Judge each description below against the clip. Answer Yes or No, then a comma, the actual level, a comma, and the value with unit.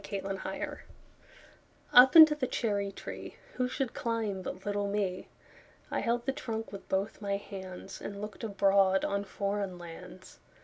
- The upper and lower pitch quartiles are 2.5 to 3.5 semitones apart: Yes, average, 2.9 semitones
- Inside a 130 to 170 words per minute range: Yes, slow, 135 wpm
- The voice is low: No, high, 200 Hz